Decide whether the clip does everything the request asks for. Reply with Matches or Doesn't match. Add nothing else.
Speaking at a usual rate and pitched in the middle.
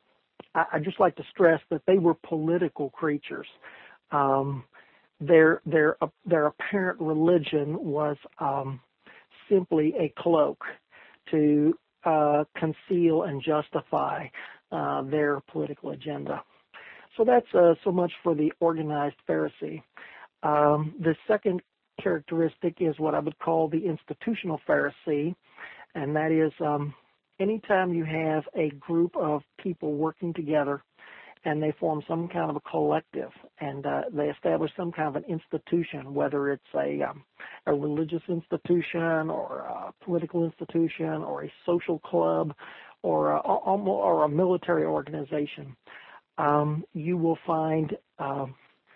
Doesn't match